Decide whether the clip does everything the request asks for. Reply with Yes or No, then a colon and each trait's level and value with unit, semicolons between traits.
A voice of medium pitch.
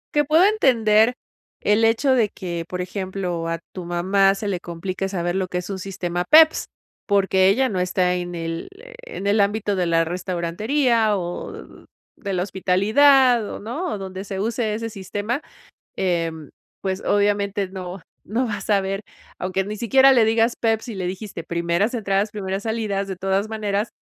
No: high, 195 Hz